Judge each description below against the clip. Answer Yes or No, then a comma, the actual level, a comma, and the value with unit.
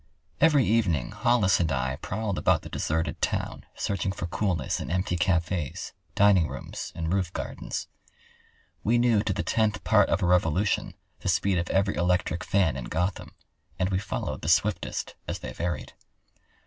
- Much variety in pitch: No, average, 3.3 semitones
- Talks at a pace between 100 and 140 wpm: No, average, 160 wpm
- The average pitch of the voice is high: No, very low, 95 Hz